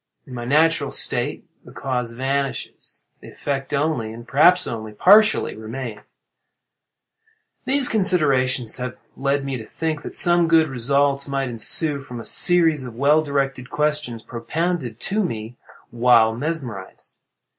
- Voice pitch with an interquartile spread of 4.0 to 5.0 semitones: Yes, average, 4.6 semitones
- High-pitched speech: No, low, 135 Hz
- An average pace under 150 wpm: Yes, slow, 135 wpm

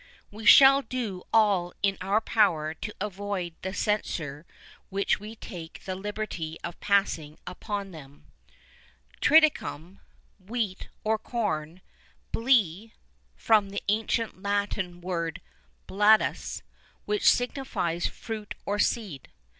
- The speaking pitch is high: Yes, high, 200 Hz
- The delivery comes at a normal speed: No, slow, 110 wpm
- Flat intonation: No, average, 3.7 semitones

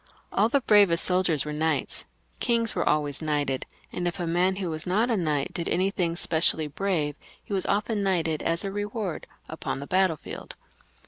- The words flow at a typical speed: Yes, average, 180 wpm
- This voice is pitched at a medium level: Yes, medium, 175 Hz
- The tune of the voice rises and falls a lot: No, average, 4.0 semitones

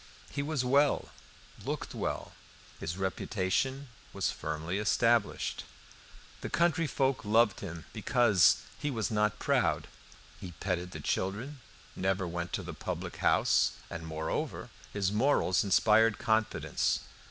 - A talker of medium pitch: No, low, 105 Hz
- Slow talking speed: Yes, slow, 125 wpm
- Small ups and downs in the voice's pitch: No, average, 5.1 semitones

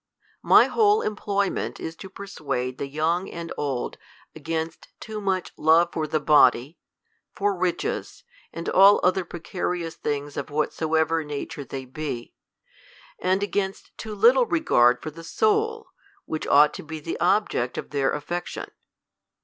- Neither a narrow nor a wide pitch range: Yes, average, 4.9 semitones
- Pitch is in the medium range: Yes, medium, 165 Hz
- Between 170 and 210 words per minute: No, average, 140 wpm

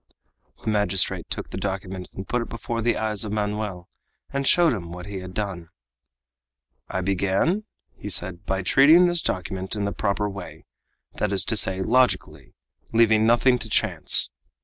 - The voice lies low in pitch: Yes, low, 100 Hz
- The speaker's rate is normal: Yes, average, 170 wpm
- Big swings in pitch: No, average, 3.6 semitones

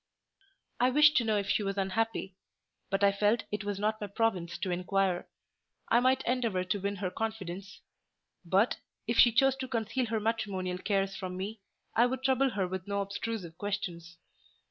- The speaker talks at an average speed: Yes, average, 180 wpm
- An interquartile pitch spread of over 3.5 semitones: No, average, 3.2 semitones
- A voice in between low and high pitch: No, high, 205 Hz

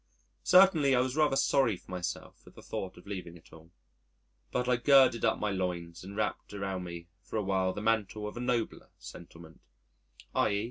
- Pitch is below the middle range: Yes, low, 100 Hz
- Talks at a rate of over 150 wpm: Yes, average, 190 wpm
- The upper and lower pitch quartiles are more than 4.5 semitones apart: Yes, wide, 5.5 semitones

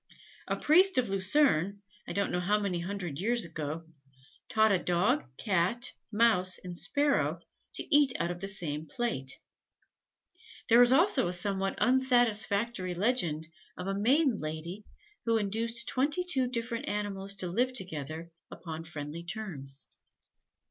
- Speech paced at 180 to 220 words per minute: No, average, 140 wpm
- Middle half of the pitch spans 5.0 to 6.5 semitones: Yes, wide, 5.6 semitones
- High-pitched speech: Yes, high, 200 Hz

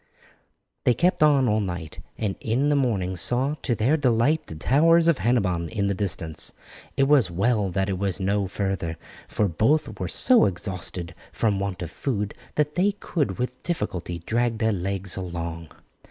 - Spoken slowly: No, average, 170 wpm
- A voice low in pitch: Yes, low, 105 Hz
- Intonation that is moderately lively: No, wide, 6.1 semitones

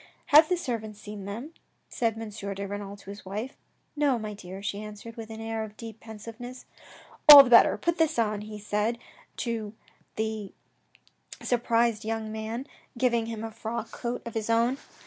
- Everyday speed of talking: No, fast, 215 wpm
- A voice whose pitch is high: Yes, high, 225 Hz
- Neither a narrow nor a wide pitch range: No, narrow, 2.0 semitones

